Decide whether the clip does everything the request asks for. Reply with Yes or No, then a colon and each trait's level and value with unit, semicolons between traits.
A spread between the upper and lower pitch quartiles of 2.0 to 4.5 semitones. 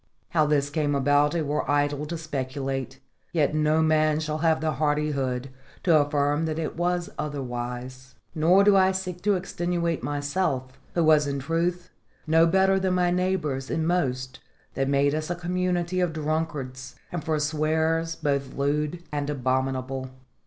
Yes: average, 3.3 semitones